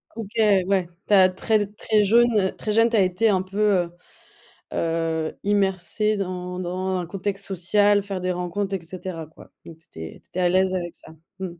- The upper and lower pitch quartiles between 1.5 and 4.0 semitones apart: Yes, narrow, 2.4 semitones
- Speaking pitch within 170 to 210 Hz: Yes, high, 190 Hz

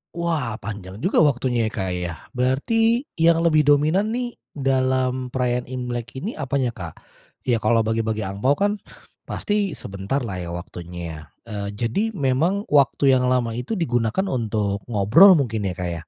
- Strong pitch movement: Yes, wide, 5.8 semitones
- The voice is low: Yes, low, 125 Hz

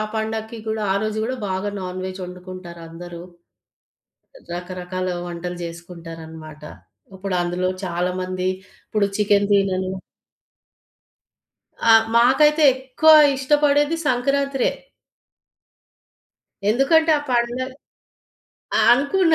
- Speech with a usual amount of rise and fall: No, wide, 6.3 semitones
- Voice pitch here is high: Yes, high, 195 Hz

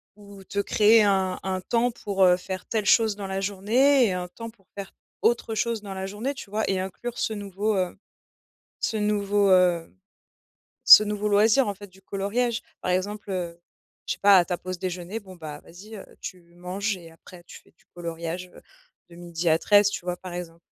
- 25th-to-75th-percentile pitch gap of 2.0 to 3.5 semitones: Yes, narrow, 2.6 semitones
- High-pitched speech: Yes, high, 195 Hz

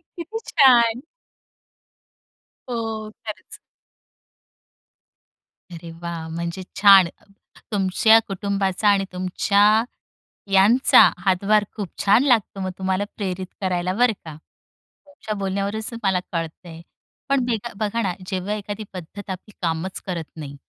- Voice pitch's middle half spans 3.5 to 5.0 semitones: No, average, 3.1 semitones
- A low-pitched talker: No, high, 195 Hz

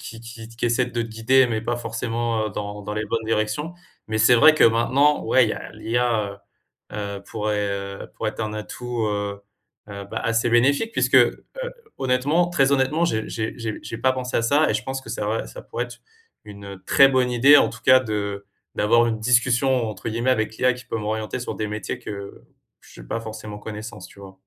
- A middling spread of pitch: Yes, average, 3.0 semitones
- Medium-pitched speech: No, low, 115 Hz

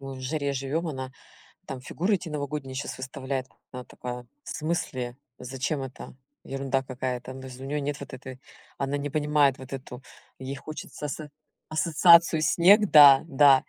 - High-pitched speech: No, low, 135 Hz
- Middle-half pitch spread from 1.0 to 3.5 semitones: Yes, narrow, 2.4 semitones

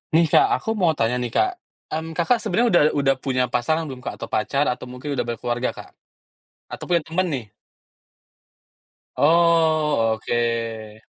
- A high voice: No, medium, 140 Hz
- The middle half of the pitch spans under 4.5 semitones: No, wide, 5.6 semitones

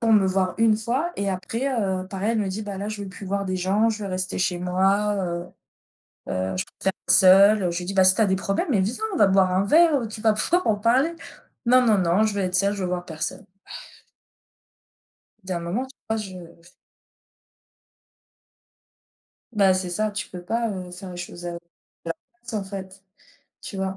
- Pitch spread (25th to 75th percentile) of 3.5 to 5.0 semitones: No, average, 2.8 semitones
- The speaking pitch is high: Yes, high, 195 Hz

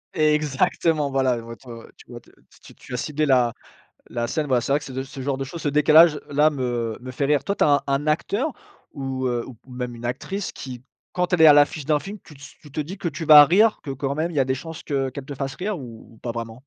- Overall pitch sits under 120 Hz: No, medium, 140 Hz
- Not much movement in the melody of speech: No, average, 3.2 semitones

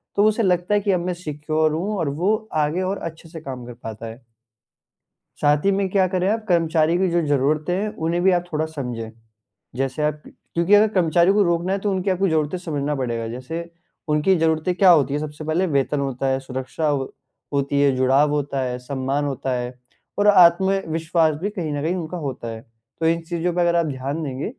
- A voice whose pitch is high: No, medium, 160 Hz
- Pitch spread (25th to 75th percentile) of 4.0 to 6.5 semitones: Yes, average, 4.4 semitones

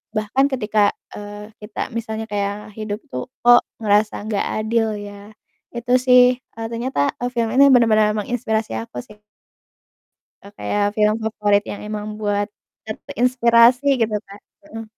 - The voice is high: Yes, high, 215 Hz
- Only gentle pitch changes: Yes, narrow, 2.2 semitones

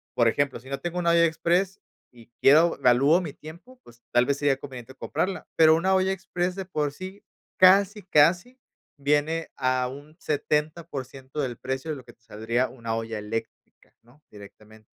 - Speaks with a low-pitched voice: No, medium, 145 Hz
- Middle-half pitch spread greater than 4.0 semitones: Yes, wide, 5.4 semitones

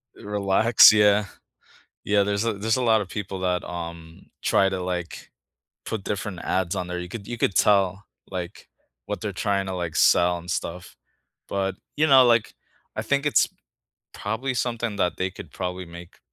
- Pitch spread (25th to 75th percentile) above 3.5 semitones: No, average, 3.2 semitones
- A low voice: Yes, very low, 95 Hz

